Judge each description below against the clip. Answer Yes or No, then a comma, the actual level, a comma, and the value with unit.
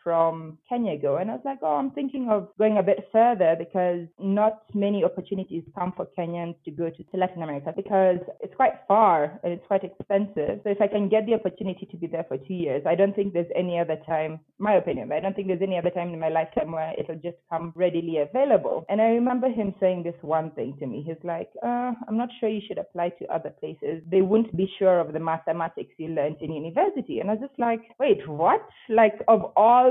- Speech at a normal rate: No, fast, 235 wpm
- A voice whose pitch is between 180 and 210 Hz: Yes, medium, 185 Hz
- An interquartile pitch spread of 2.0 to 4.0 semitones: No, average, 4.4 semitones